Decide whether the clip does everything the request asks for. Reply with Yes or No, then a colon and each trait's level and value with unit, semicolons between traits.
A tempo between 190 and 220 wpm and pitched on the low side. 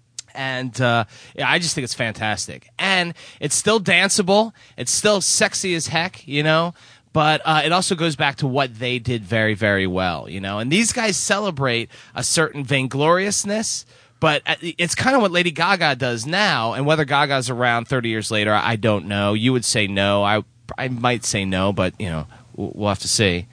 Yes: average, 195 wpm; low, 130 Hz